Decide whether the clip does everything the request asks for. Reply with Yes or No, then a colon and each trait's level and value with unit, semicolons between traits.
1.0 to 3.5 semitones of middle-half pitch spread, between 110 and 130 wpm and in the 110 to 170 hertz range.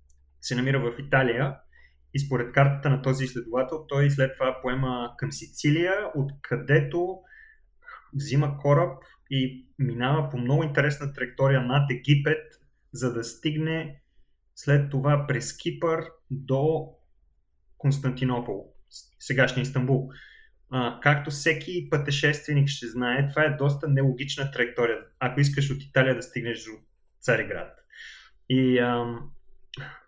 Yes: average, 3.0 semitones; average, 120 wpm; low, 135 Hz